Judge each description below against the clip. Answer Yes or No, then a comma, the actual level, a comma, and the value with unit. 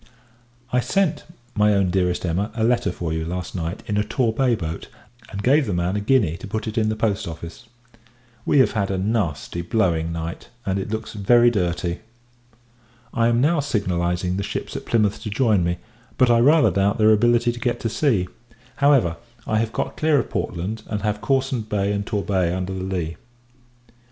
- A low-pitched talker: Yes, low, 105 Hz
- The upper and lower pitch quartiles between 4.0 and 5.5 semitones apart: Yes, average, 4.7 semitones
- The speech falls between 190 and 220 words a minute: Yes, average, 195 wpm